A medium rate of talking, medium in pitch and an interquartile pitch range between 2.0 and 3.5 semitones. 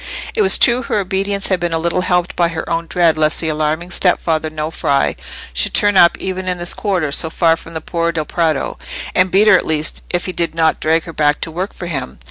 No: fast, 240 wpm; medium, 170 Hz; narrow, 2.6 semitones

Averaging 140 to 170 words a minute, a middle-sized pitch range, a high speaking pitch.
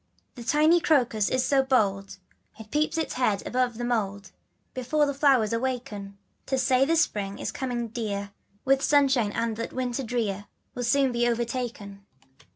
Yes: average, 165 wpm; average, 3.8 semitones; high, 245 Hz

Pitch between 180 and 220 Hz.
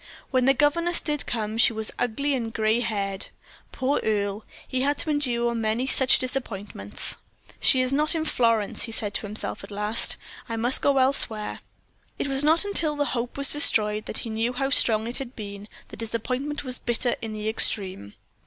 No: high, 235 Hz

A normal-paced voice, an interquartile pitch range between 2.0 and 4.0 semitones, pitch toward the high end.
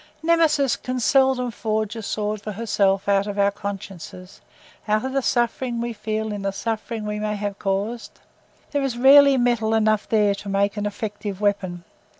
Yes: average, 170 wpm; average, 2.9 semitones; high, 215 Hz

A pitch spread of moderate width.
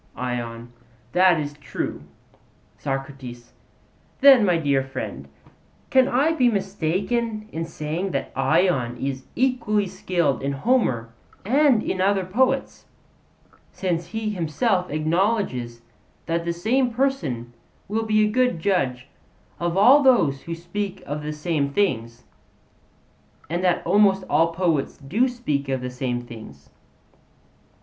No: wide, 7.7 semitones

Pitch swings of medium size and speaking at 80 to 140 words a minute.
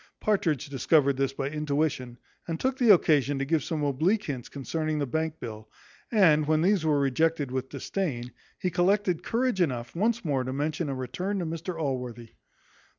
No: average, 4.7 semitones; average, 175 wpm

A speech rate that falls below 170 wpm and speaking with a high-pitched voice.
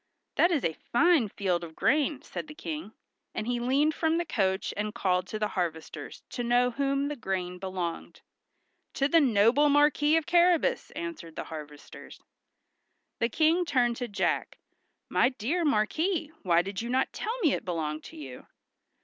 No: average, 175 wpm; high, 245 Hz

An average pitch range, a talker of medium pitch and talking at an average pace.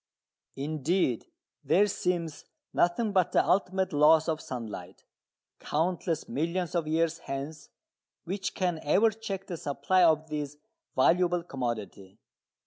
No: average, 3.7 semitones; medium, 165 Hz; slow, 120 wpm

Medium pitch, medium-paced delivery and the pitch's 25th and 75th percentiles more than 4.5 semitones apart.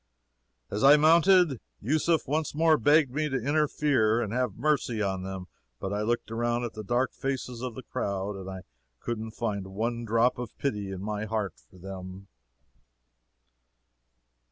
No: low, 115 Hz; average, 160 wpm; average, 5.3 semitones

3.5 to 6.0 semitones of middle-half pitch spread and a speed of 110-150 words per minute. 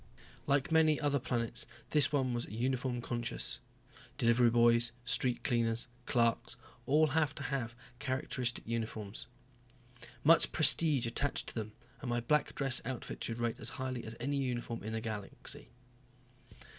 No: average, 2.9 semitones; average, 145 wpm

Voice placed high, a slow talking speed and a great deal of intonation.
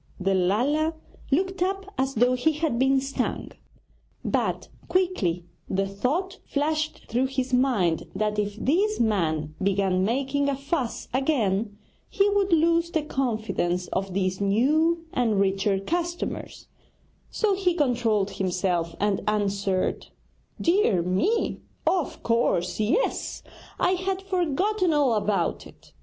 Yes: very high, 255 Hz; slow, 125 wpm; wide, 8.9 semitones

